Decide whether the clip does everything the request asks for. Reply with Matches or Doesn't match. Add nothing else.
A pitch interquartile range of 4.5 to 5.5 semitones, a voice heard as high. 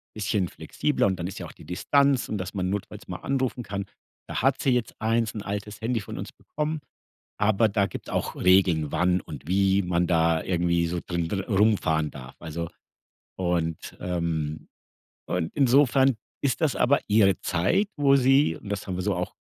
Doesn't match